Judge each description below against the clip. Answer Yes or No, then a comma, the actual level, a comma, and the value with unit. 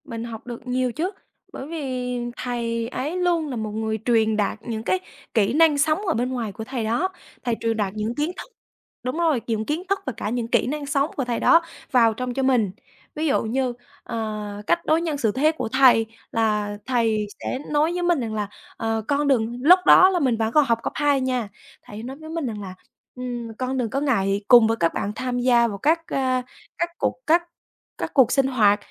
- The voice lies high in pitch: Yes, very high, 250 Hz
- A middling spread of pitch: Yes, average, 4.4 semitones